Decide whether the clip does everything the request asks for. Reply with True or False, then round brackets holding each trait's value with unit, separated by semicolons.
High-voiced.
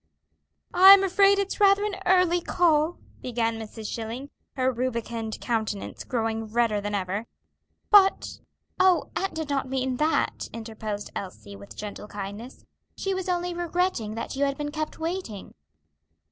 True (260 Hz)